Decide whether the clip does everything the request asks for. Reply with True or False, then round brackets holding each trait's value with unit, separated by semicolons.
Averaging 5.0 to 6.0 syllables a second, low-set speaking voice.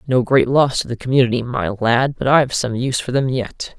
True (5.6 syllables/s; 130 Hz)